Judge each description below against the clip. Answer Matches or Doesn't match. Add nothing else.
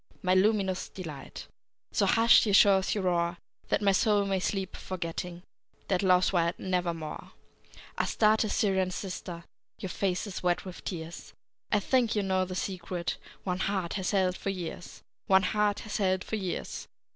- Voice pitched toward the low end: Doesn't match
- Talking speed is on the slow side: Doesn't match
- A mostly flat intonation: Matches